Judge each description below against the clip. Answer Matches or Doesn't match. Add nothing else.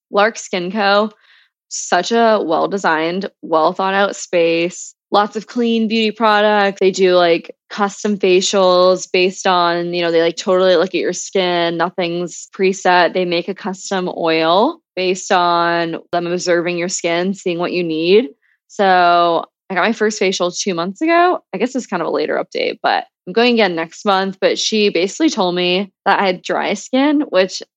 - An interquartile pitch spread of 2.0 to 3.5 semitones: Matches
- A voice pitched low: Doesn't match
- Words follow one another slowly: Doesn't match